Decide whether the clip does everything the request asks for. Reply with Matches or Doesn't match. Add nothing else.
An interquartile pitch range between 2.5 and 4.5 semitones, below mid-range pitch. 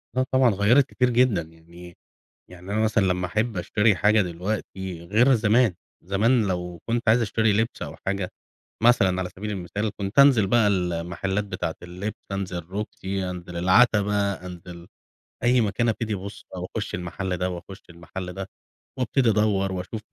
Matches